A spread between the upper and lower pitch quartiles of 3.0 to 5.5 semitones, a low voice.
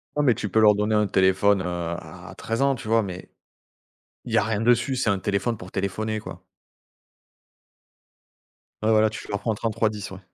No: narrow, 2.4 semitones; low, 105 Hz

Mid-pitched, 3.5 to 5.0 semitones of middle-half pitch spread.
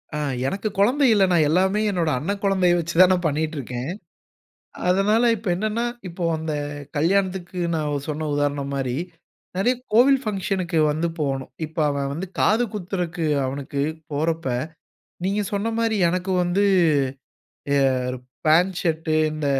Yes: medium, 175 Hz; average, 4.6 semitones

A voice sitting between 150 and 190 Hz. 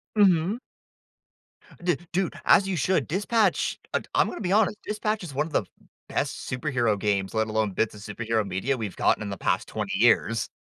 No: low, 130 Hz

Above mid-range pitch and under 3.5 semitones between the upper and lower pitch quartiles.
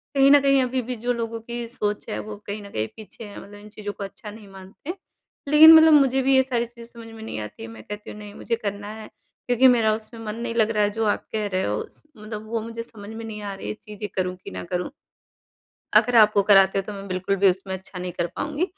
Yes: high, 215 Hz; average, 2.9 semitones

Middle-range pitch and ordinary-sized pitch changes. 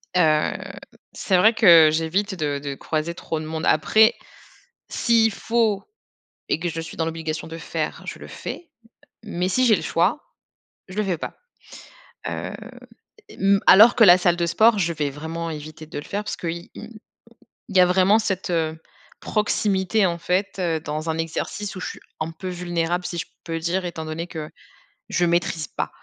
Yes: medium, 175 Hz; average, 3.5 semitones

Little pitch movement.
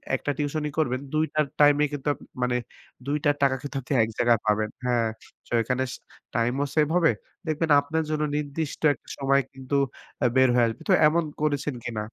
No: average, 3.5 semitones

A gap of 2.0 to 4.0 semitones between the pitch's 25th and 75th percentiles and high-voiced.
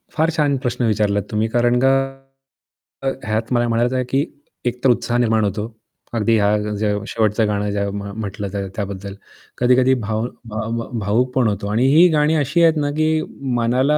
No: average, 3.7 semitones; low, 115 Hz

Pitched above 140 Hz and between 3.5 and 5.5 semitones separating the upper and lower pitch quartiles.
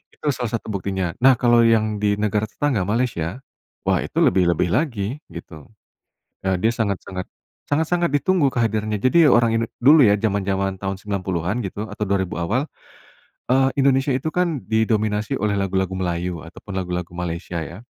No: low, 105 Hz; average, 4.6 semitones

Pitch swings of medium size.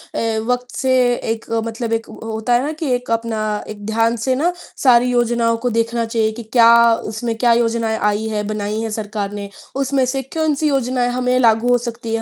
No: narrow, 2.0 semitones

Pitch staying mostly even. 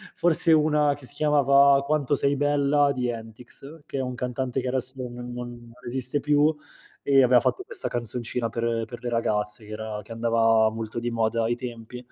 No: average, 3.4 semitones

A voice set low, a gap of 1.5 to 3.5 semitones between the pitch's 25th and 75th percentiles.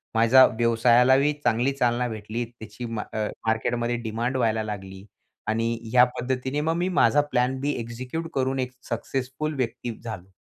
Yes: low, 120 Hz; narrow, 2.6 semitones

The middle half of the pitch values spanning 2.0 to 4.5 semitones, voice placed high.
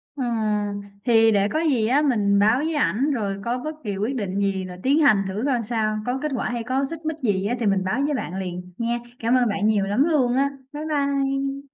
No: average, 5.2 semitones; high, 235 Hz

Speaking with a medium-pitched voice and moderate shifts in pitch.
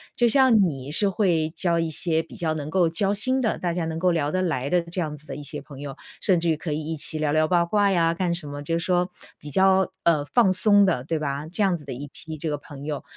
Yes: medium, 165 Hz; average, 3.7 semitones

